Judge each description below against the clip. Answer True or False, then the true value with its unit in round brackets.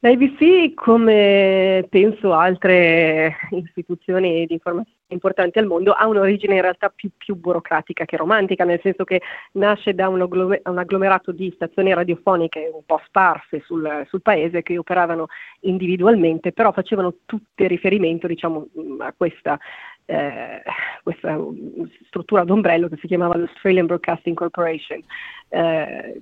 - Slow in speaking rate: False (130 wpm)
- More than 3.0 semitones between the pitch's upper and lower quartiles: False (2.6 semitones)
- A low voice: False (185 Hz)